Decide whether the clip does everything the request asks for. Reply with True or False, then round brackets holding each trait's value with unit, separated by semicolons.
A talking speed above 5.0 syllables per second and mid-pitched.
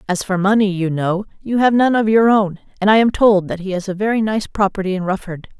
False (5.8 syllables/s; 200 Hz)